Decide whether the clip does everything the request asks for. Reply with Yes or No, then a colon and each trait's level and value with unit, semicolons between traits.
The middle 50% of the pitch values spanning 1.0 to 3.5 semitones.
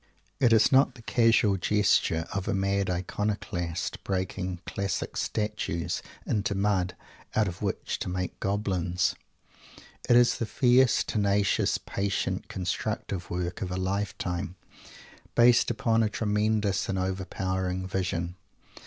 Yes: narrow, 2.5 semitones